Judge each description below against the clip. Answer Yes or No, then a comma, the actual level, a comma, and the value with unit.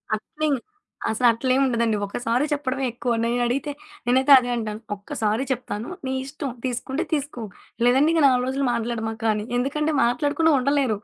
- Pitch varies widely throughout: No, average, 3.2 semitones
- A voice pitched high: Yes, very high, 250 Hz